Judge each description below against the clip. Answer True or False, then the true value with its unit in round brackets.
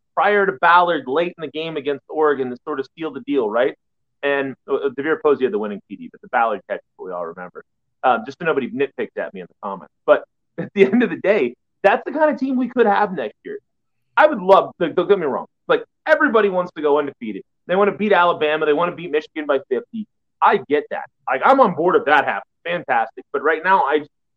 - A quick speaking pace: True (245 wpm)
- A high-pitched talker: True (195 Hz)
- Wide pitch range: True (8.9 semitones)